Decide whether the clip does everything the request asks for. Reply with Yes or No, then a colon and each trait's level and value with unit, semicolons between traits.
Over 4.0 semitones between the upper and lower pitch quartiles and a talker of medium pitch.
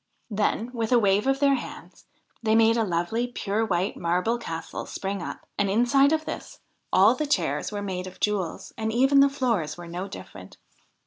No: average, 4.9 semitones; high, 215 Hz